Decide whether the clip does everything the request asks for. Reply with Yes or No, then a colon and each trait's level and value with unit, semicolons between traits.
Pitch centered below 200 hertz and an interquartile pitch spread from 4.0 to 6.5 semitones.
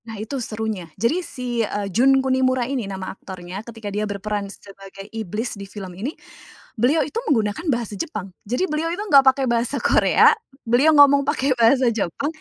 No: high, 235 Hz; average, 4.9 semitones